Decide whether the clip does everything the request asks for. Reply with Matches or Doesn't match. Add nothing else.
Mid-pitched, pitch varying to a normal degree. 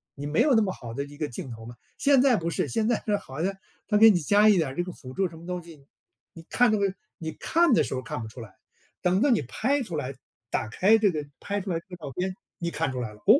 Doesn't match